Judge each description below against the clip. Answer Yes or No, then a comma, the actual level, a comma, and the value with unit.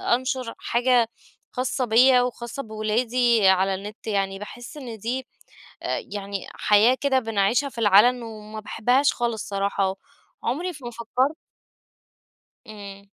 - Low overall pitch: No, high, 230 Hz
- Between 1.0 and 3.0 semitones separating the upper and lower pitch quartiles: No, average, 3.4 semitones